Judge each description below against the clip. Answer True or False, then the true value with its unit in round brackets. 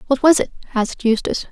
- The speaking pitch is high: True (250 Hz)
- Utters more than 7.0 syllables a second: True (7.3 syllables/s)